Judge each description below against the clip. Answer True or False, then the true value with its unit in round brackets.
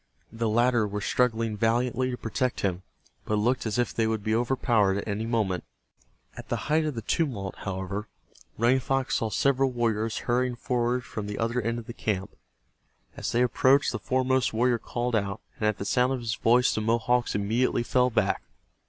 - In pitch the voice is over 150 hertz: False (115 Hz)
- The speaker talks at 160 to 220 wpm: True (195 wpm)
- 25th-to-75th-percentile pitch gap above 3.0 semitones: False (2.6 semitones)